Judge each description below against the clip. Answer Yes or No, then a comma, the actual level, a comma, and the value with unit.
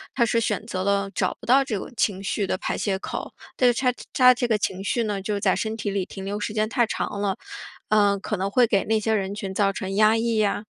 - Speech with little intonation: Yes, narrow, 2.3 semitones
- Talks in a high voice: Yes, high, 210 Hz